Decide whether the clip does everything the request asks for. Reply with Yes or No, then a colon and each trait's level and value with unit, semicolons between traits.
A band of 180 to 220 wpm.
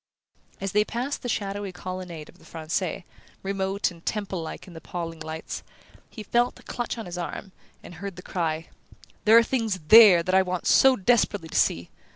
Yes: average, 190 wpm